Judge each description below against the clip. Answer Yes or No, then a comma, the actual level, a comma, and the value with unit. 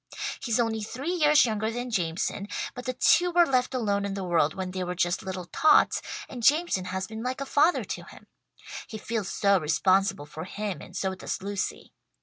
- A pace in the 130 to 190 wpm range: No, average, 200 wpm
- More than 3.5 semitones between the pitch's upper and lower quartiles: Yes, average, 5.1 semitones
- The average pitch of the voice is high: Yes, high, 205 Hz